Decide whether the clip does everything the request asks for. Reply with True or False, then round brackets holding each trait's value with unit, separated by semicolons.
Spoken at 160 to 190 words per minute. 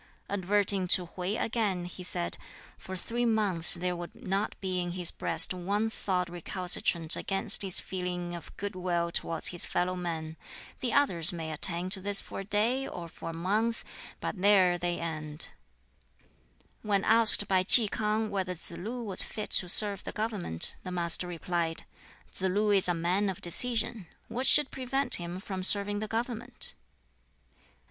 True (170 wpm)